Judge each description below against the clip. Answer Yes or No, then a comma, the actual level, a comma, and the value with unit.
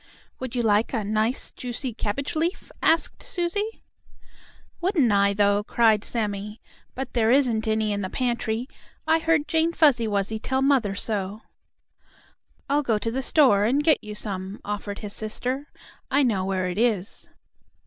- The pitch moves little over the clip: No, average, 4.8 semitones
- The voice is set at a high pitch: Yes, high, 225 Hz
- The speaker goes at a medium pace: Yes, average, 160 wpm